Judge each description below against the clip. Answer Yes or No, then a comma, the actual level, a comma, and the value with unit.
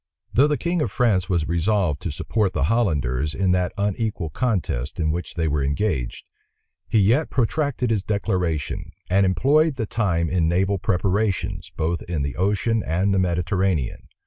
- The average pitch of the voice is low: Yes, very low, 95 Hz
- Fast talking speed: No, average, 165 wpm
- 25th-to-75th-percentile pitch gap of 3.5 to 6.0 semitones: Yes, average, 4.6 semitones